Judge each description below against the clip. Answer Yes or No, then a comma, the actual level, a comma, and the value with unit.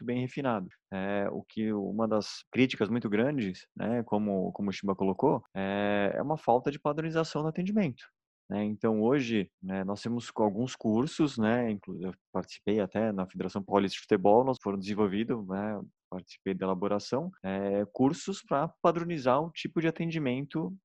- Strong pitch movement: Yes, wide, 6.2 semitones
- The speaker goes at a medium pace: Yes, average, 165 wpm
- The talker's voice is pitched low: Yes, low, 110 Hz